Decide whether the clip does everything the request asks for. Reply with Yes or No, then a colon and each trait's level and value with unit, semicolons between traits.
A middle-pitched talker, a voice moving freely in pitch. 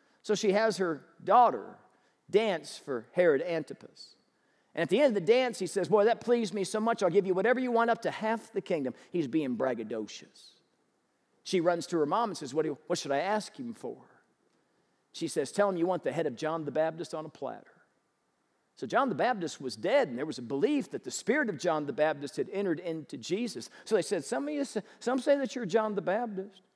No: high, 195 Hz; wide, 6.3 semitones